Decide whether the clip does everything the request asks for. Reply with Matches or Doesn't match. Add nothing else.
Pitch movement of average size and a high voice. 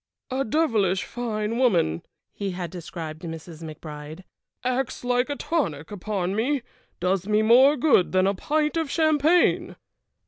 Doesn't match